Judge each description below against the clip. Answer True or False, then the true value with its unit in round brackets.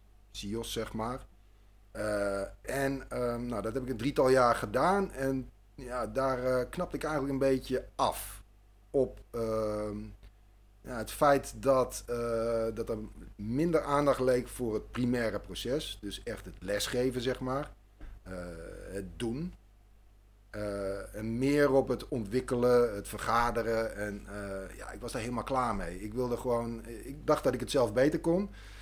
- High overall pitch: False (115 Hz)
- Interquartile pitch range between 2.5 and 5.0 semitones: True (3.9 semitones)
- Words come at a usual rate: True (160 wpm)